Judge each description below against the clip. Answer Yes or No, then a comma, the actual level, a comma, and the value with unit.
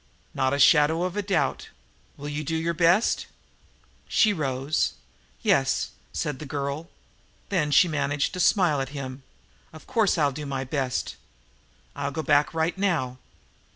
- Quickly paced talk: No, average, 155 wpm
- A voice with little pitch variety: No, average, 3.3 semitones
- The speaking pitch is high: No, medium, 150 Hz